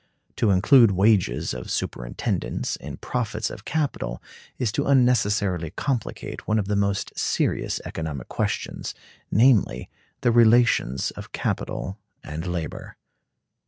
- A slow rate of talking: Yes, slow, 115 wpm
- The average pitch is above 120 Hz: No, low, 105 Hz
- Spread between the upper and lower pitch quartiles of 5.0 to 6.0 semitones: Yes, average, 5.3 semitones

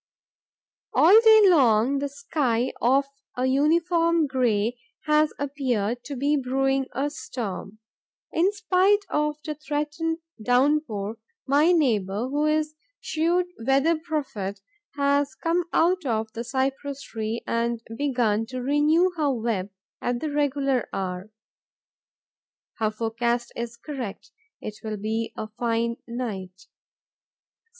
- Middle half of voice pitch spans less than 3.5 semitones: No, average, 4.8 semitones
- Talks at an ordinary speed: No, slow, 125 wpm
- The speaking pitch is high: Yes, very high, 270 Hz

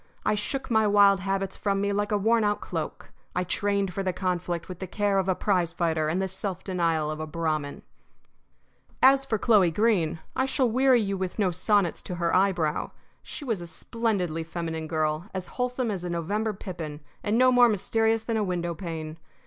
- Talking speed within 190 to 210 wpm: Yes, average, 200 wpm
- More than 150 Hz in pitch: Yes, high, 190 Hz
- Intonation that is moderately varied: Yes, average, 3.9 semitones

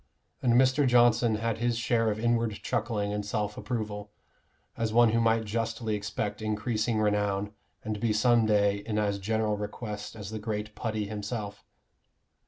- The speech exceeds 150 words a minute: Yes, average, 160 wpm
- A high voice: No, low, 110 Hz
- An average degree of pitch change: No, narrow, 1.8 semitones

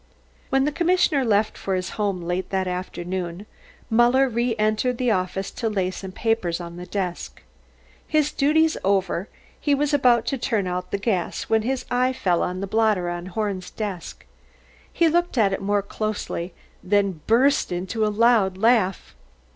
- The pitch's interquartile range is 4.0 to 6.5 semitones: Yes, average, 4.8 semitones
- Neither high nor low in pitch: No, high, 210 Hz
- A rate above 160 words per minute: Yes, average, 170 wpm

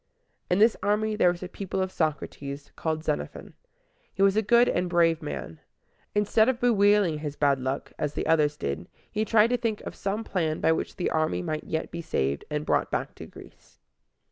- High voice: No, medium, 170 Hz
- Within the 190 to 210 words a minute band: Yes, average, 200 wpm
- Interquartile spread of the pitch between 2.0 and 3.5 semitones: No, wide, 5.6 semitones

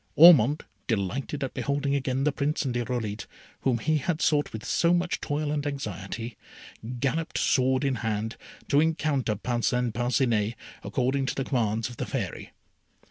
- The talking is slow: No, average, 155 wpm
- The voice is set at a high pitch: No, low, 130 Hz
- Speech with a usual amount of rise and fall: Yes, average, 3.8 semitones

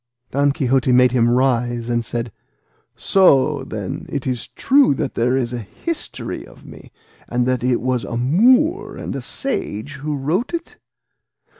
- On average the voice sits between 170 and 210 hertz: No, low, 130 Hz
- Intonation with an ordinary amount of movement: Yes, average, 3.8 semitones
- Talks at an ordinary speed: Yes, average, 160 wpm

